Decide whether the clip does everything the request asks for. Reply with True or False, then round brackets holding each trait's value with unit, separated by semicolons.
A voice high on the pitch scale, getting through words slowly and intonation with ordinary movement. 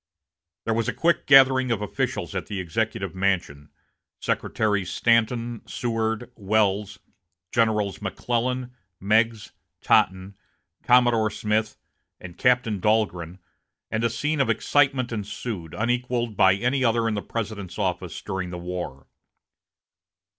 False (110 Hz; 120 wpm; 3.6 semitones)